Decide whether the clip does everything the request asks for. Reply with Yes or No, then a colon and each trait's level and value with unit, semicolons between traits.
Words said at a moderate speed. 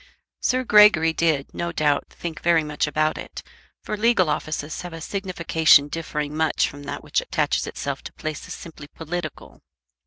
Yes: average, 160 wpm